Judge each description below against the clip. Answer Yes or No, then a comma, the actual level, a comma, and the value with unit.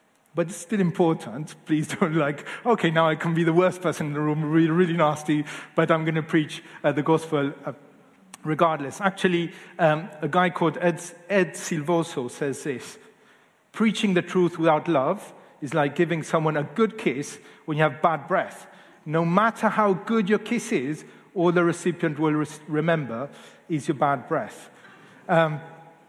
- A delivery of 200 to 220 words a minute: No, average, 175 wpm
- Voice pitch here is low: No, medium, 165 Hz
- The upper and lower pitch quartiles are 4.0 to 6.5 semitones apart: No, average, 2.7 semitones